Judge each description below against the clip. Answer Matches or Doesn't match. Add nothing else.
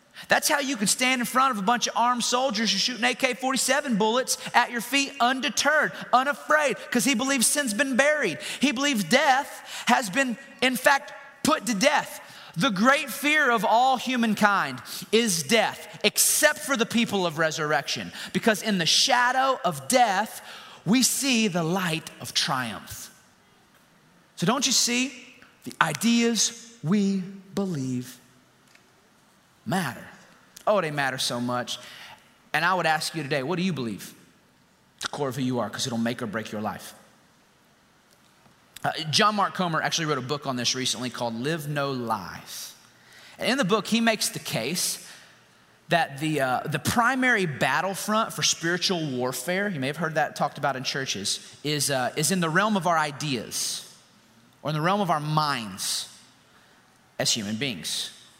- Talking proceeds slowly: Doesn't match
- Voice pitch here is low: Doesn't match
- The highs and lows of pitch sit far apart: Matches